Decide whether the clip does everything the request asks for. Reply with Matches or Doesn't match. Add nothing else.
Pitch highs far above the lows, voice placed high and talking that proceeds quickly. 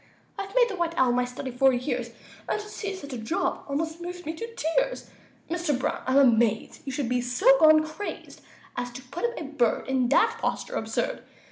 Matches